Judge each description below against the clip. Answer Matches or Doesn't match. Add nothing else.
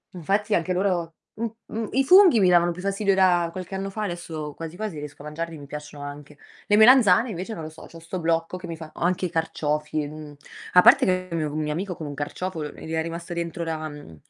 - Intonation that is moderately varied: Matches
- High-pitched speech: Doesn't match